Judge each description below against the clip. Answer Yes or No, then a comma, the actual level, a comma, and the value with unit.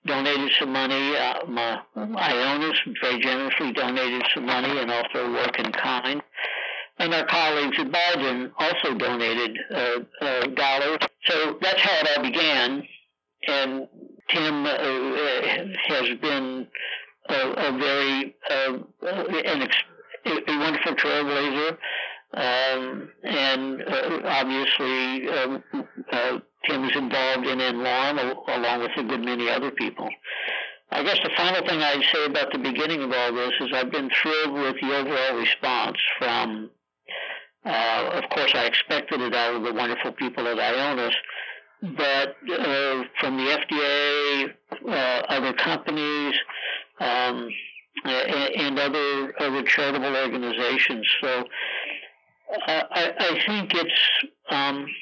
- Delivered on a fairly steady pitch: Yes, narrow, 2.2 semitones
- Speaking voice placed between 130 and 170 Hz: Yes, low, 135 Hz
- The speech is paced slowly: Yes, slow, 130 wpm